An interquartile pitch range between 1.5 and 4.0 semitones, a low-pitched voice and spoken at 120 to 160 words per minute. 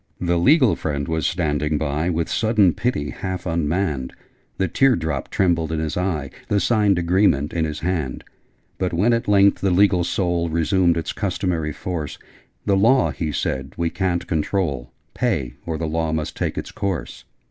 No: average, 3.7 semitones; very low, 85 Hz; average, 170 wpm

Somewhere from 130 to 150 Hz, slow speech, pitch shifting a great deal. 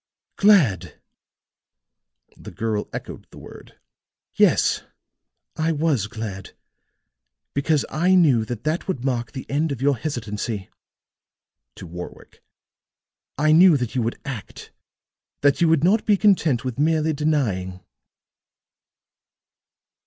Yes: medium, 140 Hz; slow, 115 wpm; wide, 6.0 semitones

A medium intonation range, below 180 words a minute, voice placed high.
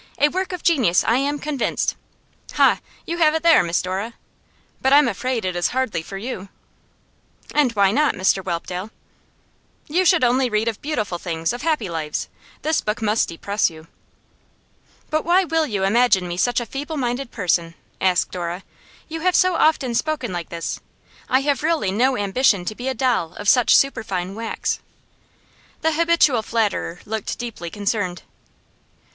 No: wide, 7.4 semitones; average, 165 wpm; high, 230 Hz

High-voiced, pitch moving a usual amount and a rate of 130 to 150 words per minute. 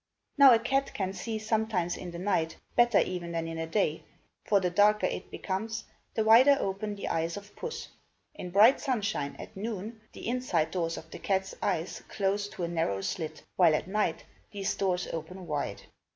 No: high, 195 Hz; average, 4.3 semitones; average, 190 wpm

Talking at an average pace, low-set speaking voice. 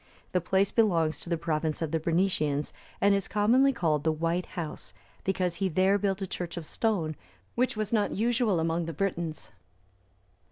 No: average, 175 wpm; medium, 180 Hz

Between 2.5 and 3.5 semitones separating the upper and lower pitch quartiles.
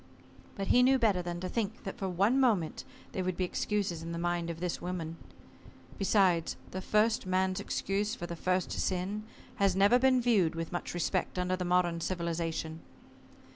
Yes: average, 3.0 semitones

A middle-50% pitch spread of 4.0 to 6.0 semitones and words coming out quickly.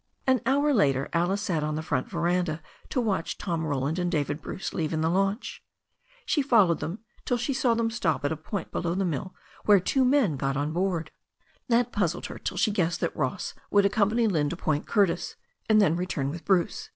Yes: average, 5.3 semitones; fast, 210 wpm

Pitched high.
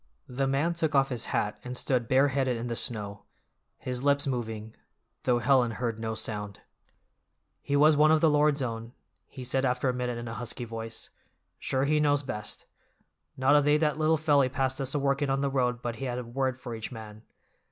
No: low, 130 Hz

